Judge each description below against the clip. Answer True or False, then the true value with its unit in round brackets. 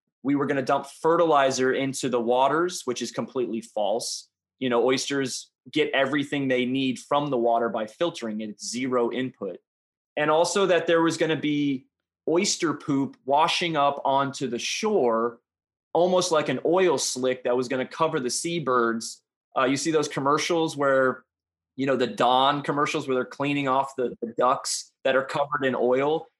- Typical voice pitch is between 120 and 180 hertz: True (135 Hz)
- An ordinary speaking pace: True (180 wpm)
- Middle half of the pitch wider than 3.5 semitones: False (3.1 semitones)